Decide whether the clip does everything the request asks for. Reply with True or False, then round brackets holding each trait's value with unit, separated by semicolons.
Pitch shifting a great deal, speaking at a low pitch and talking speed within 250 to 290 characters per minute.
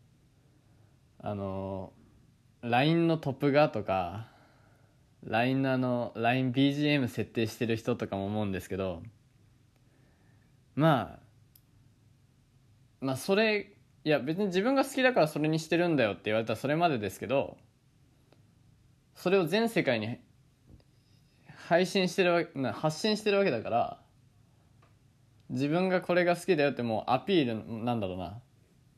False (4.2 semitones; 130 Hz; 260 characters per minute)